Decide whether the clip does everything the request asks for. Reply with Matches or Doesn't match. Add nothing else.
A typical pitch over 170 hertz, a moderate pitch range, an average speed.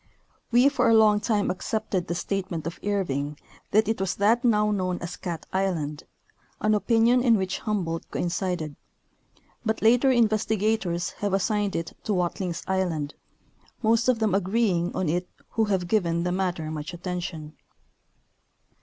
Matches